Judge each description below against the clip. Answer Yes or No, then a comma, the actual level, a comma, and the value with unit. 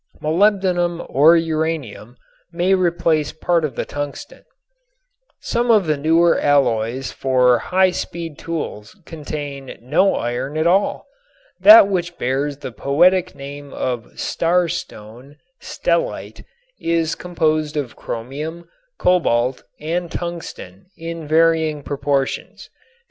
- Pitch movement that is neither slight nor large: Yes, average, 3.8 semitones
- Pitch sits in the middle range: Yes, medium, 155 Hz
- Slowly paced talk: Yes, slow, 110 wpm